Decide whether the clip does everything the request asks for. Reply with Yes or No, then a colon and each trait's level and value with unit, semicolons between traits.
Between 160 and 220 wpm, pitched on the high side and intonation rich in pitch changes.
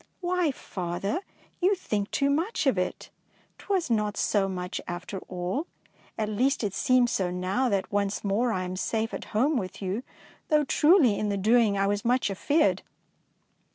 Yes: average, 175 wpm; high, 210 Hz; wide, 5.9 semitones